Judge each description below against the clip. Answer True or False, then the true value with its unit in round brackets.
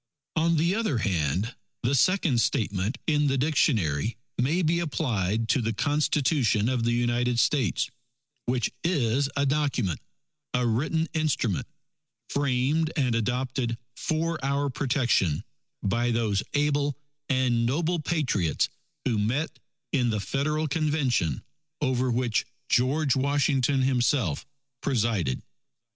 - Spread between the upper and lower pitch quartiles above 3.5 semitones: True (4.2 semitones)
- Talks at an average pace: False (120 wpm)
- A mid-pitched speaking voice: False (130 Hz)